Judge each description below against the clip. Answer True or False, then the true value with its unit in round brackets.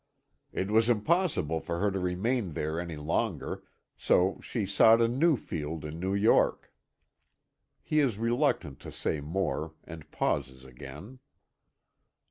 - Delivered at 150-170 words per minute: False (135 wpm)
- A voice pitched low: True (95 Hz)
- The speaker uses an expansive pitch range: True (6.7 semitones)